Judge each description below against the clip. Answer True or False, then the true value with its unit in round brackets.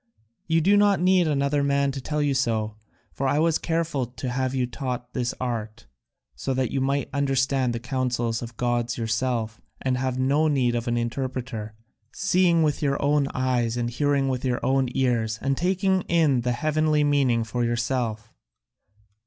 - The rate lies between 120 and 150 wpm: False (175 wpm)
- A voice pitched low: True (130 Hz)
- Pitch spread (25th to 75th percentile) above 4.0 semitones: False (3.2 semitones)